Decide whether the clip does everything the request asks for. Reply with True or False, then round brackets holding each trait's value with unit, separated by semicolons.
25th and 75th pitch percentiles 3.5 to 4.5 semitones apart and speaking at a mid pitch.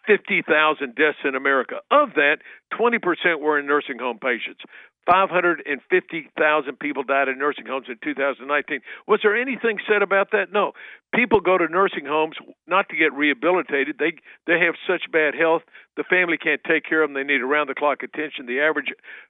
False (5.1 semitones; 155 Hz)